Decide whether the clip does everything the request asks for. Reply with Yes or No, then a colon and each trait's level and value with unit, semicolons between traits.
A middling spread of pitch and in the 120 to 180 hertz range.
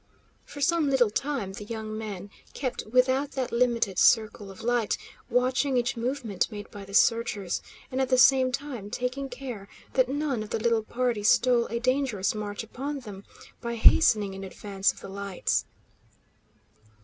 No: average, 3.8 semitones; high, 235 Hz